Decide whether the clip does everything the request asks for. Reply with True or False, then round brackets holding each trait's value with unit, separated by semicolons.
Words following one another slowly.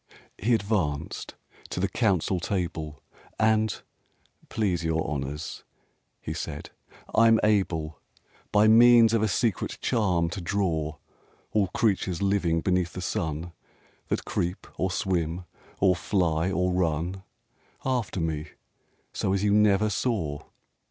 True (125 wpm)